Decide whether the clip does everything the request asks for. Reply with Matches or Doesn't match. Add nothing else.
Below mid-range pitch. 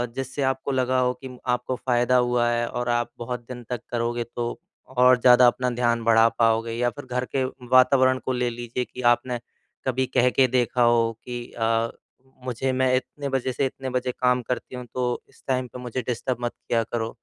Matches